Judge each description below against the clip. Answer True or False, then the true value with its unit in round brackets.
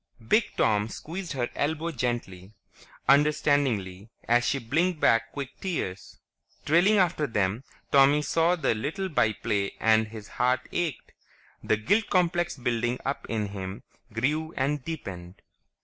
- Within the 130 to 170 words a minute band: True (135 wpm)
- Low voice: True (130 Hz)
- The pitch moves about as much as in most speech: False (6.5 semitones)